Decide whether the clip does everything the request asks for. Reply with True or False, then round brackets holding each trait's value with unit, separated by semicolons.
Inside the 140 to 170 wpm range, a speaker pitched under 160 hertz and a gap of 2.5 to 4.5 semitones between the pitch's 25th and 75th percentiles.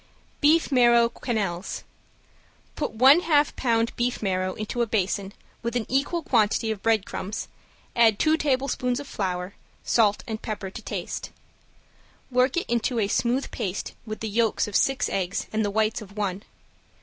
False (160 wpm; 225 Hz; 3.6 semitones)